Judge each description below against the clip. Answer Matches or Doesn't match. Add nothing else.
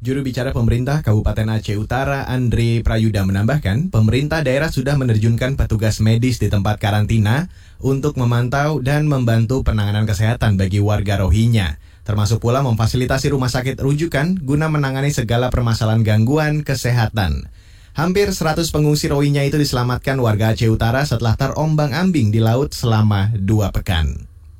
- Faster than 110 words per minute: Matches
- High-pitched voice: Doesn't match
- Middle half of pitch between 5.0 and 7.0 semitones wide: Doesn't match